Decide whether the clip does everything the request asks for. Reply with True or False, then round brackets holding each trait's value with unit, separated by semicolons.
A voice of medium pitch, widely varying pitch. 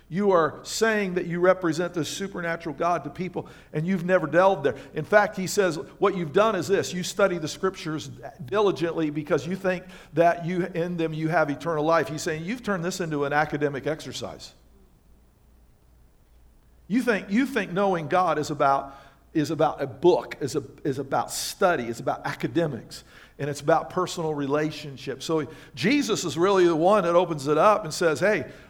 False (165 Hz; 3.6 semitones)